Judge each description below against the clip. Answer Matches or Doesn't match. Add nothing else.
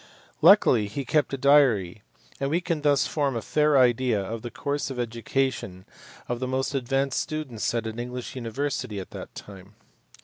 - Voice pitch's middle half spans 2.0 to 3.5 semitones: Doesn't match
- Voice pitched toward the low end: Matches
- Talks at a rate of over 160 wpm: Matches